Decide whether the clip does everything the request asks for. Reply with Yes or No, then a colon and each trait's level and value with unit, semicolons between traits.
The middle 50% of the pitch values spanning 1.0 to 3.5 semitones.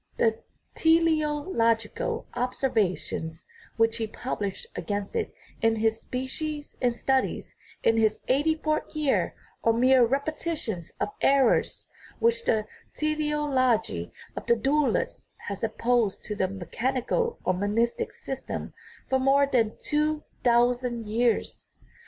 No: average, 5.0 semitones